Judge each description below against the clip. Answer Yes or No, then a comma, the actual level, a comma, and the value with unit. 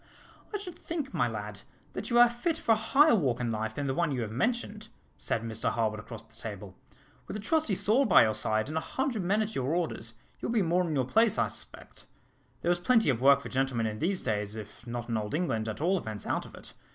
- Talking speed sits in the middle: No, fast, 250 wpm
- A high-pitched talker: No, medium, 145 Hz